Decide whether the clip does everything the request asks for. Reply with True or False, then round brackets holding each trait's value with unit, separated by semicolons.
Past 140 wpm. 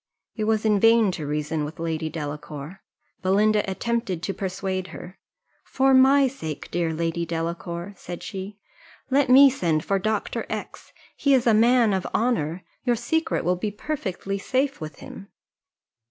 True (155 wpm)